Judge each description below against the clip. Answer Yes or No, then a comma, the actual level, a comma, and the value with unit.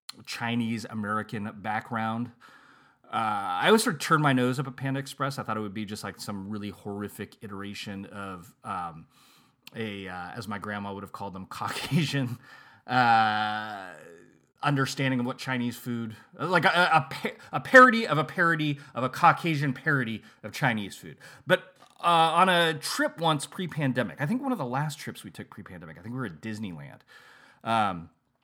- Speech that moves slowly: No, average, 175 wpm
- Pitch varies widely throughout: Yes, wide, 6.0 semitones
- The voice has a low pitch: Yes, low, 120 Hz